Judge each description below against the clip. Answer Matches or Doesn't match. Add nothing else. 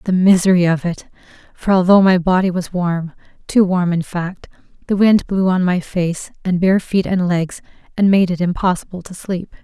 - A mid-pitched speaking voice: Matches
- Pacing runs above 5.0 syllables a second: Doesn't match